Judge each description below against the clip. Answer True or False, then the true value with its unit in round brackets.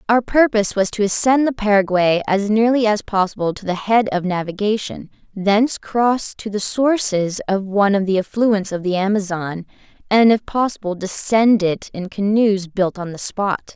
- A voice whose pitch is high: True (205 Hz)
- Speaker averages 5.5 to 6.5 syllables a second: False (4.8 syllables/s)